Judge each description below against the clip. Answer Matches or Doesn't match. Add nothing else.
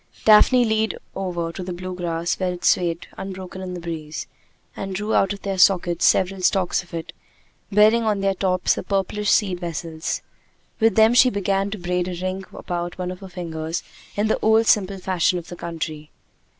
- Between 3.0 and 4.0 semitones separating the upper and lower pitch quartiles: Doesn't match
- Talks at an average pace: Matches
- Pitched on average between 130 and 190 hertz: Matches